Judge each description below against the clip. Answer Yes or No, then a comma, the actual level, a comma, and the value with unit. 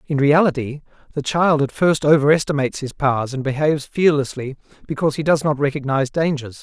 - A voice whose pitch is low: No, medium, 145 Hz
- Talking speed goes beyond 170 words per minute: No, average, 165 wpm